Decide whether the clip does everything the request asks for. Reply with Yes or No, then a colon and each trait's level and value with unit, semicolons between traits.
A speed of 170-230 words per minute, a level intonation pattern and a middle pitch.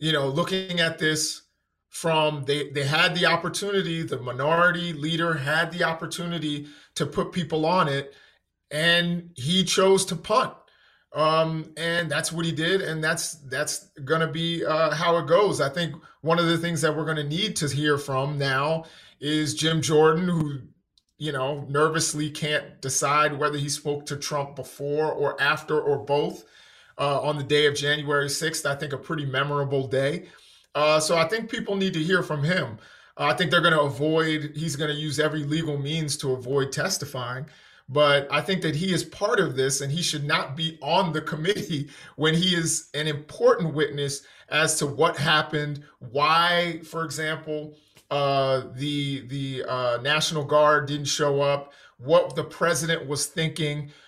Yes: average, 175 wpm; narrow, 2.3 semitones; medium, 155 Hz